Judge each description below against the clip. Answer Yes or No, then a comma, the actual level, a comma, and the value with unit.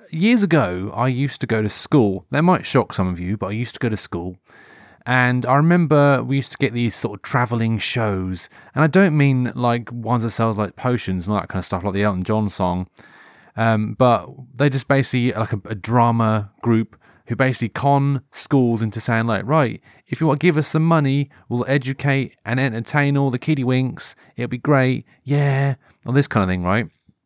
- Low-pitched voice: Yes, low, 120 Hz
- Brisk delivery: Yes, fast, 215 wpm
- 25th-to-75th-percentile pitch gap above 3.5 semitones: Yes, average, 4.0 semitones